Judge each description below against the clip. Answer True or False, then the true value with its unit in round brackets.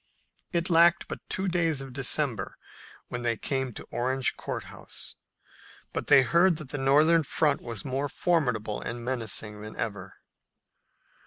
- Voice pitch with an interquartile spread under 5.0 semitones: False (5.4 semitones)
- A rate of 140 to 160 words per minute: True (150 wpm)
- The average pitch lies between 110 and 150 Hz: True (135 Hz)